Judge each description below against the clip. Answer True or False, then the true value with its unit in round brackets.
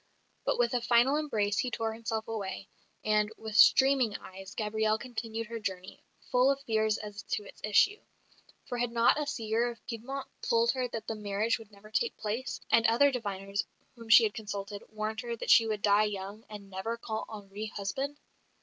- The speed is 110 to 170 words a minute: False (190 wpm)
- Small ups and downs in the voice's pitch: True (2.3 semitones)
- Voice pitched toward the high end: True (220 Hz)